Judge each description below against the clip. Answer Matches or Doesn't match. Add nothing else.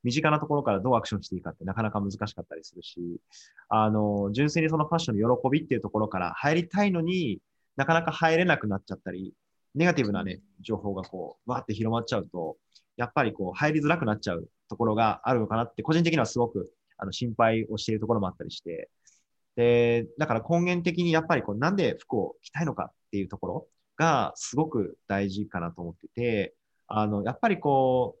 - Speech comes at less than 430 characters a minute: Doesn't match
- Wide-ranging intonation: Matches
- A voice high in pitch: Doesn't match